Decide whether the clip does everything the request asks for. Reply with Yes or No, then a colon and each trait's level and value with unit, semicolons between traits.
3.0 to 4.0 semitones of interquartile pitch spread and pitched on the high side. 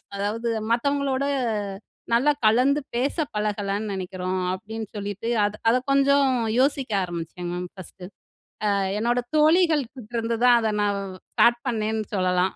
No: average, 4.6 semitones; high, 220 Hz